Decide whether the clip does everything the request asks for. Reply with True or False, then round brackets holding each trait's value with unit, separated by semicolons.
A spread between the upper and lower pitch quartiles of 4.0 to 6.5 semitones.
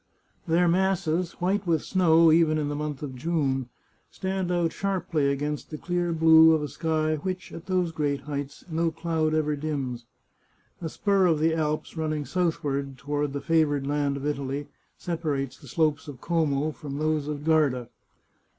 False (2.5 semitones)